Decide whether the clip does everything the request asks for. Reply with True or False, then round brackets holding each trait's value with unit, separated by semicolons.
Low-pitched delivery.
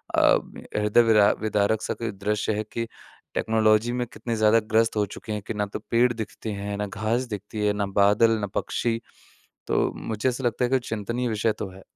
True (110 Hz)